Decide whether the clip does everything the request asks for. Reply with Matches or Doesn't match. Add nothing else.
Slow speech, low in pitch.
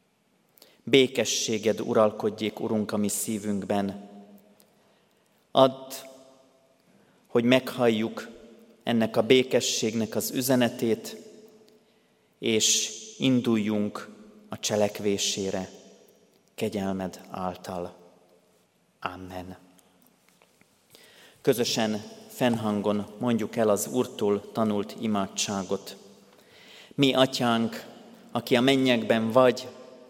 Matches